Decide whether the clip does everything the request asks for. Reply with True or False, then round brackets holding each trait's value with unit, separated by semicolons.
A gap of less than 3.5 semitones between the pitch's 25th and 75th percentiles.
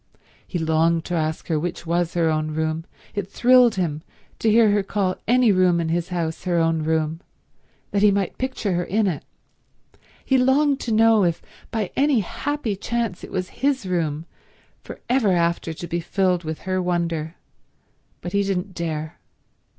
False (4.4 semitones)